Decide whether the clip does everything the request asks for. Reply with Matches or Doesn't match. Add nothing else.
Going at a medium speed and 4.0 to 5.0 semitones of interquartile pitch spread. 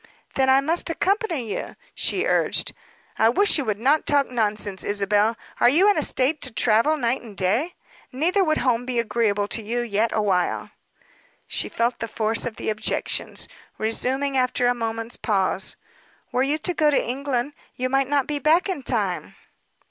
Matches